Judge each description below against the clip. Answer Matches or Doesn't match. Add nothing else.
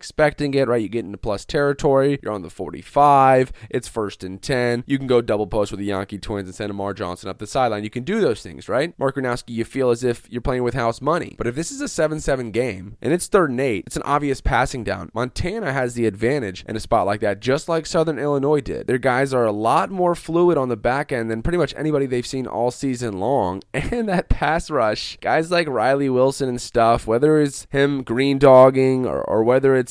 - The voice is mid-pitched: Doesn't match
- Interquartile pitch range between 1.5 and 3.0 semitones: Doesn't match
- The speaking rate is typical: Doesn't match